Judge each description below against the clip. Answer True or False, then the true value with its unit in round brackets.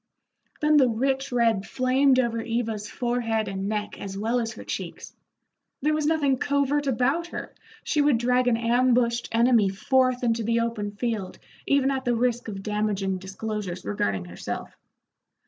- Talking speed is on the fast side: False (160 wpm)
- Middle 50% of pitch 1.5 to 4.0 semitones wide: True (3.5 semitones)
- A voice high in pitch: True (235 Hz)